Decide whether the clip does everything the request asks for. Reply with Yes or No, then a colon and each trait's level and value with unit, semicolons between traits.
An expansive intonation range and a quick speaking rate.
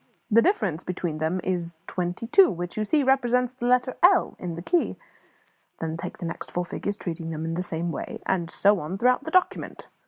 Yes: wide, 6.9 semitones; fast, 210 wpm